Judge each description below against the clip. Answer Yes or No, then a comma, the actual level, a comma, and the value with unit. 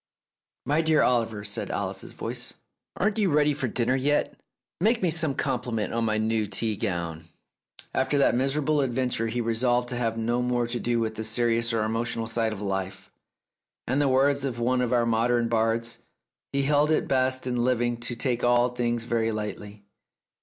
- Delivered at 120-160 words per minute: No, average, 190 wpm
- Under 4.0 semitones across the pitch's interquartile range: Yes, narrow, 2.6 semitones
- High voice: No, low, 120 Hz